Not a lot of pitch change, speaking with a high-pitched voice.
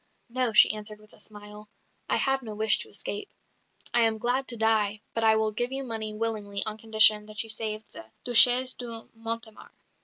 Yes: narrow, 1.5 semitones; high, 220 Hz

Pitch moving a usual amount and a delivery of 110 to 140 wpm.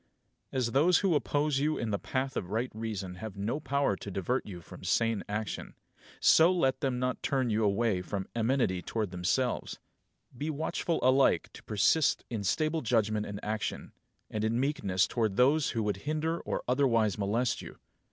No: average, 4.9 semitones; average, 180 wpm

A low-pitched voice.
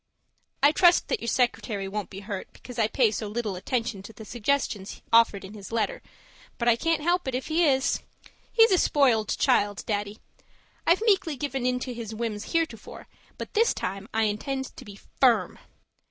No: high, 235 Hz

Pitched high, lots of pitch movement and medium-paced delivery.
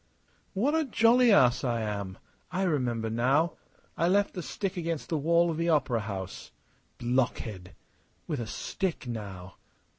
No: medium, 140 Hz; wide, 7.7 semitones; average, 150 wpm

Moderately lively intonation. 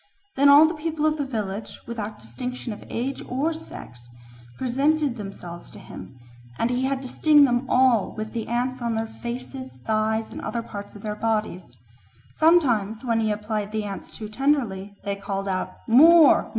Yes: average, 4.3 semitones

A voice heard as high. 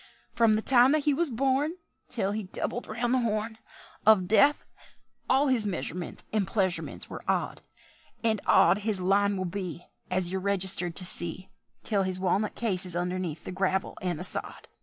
Yes: high, 200 Hz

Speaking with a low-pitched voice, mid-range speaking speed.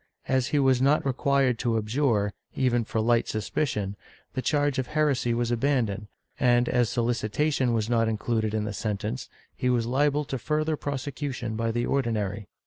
Yes: low, 120 Hz; average, 170 wpm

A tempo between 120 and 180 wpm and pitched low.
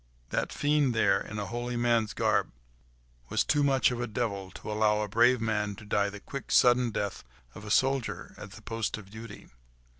No: average, 200 wpm; low, 115 Hz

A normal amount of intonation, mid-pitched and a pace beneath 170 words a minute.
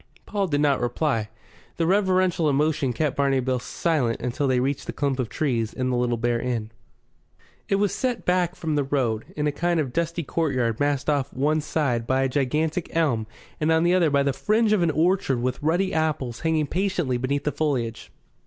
No: average, 4.3 semitones; medium, 145 Hz; fast, 205 wpm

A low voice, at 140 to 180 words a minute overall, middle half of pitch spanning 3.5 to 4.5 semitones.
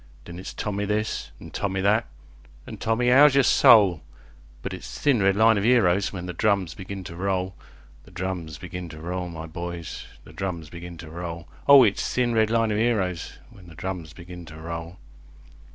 No: very low, 95 Hz; average, 190 wpm; average, 4.0 semitones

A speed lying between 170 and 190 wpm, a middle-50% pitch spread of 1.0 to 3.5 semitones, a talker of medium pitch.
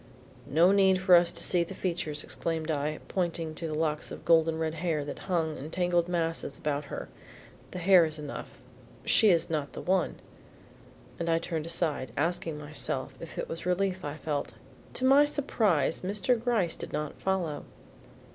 Yes: average, 175 wpm; average, 2.9 semitones; medium, 165 Hz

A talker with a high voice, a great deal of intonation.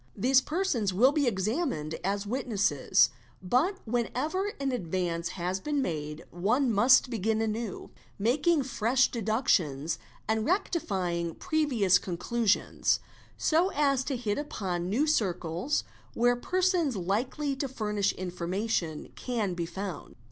Yes: high, 220 Hz; wide, 6.6 semitones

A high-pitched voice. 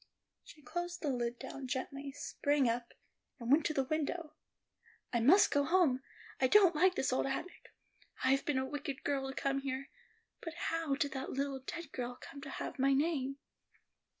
Yes: very high, 275 Hz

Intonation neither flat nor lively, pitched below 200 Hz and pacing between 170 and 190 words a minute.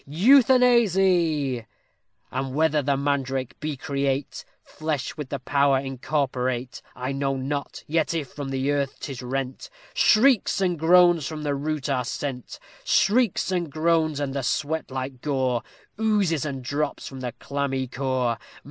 No: average, 3.3 semitones; medium, 140 Hz; average, 145 wpm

